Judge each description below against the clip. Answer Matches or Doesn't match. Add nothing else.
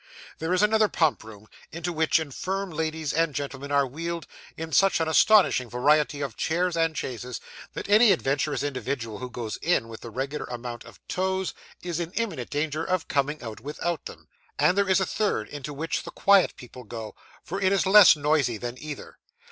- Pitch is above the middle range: Doesn't match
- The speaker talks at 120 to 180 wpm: Doesn't match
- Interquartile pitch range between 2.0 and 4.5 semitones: Doesn't match